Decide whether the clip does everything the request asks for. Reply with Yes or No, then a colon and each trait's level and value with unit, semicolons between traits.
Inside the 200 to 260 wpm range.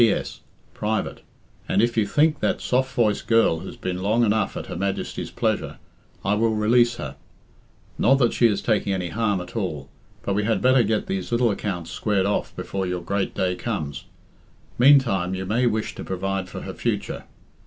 No: average, 190 wpm